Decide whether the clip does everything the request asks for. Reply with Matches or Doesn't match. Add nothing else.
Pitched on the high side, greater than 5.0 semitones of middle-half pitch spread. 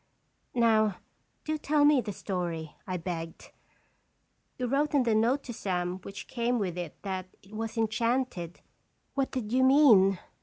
Matches